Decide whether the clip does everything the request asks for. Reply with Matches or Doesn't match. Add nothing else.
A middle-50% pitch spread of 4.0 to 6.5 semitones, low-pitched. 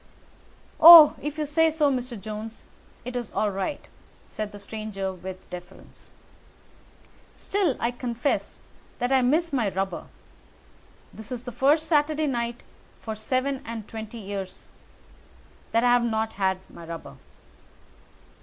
Doesn't match